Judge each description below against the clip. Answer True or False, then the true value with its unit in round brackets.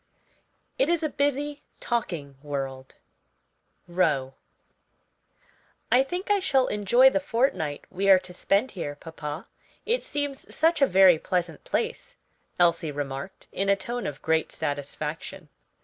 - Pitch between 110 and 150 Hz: False (185 Hz)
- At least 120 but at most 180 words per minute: True (135 wpm)